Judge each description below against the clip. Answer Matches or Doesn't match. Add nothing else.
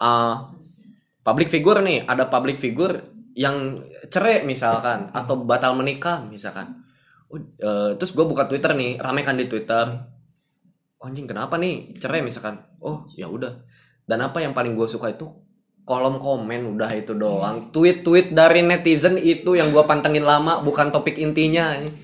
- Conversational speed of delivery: Doesn't match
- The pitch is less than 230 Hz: Matches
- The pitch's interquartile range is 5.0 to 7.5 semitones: Matches